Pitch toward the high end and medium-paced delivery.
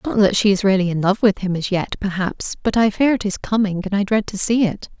No: high, 200 Hz; fast, 290 wpm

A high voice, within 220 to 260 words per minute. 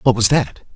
No: low, 120 Hz; fast, 235 wpm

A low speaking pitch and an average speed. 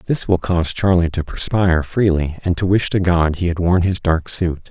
No: very low, 90 Hz; fast, 230 wpm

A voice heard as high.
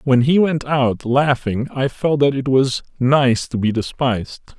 No: low, 130 Hz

